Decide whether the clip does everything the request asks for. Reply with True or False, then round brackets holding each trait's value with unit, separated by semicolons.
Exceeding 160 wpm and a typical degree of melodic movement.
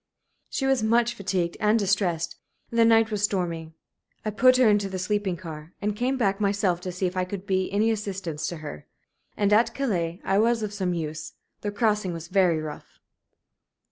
True (195 wpm; 3.5 semitones)